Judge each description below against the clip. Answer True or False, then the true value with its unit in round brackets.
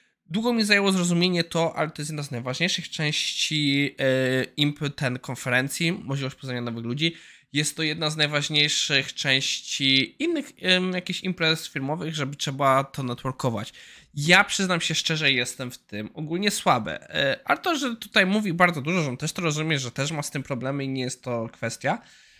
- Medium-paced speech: False (175 wpm)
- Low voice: False (150 Hz)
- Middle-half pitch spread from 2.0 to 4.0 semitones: False (4.7 semitones)